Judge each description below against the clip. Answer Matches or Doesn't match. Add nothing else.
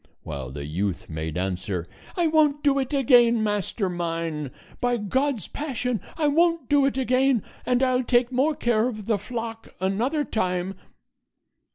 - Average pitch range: Doesn't match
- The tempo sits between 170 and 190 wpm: Doesn't match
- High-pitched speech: Matches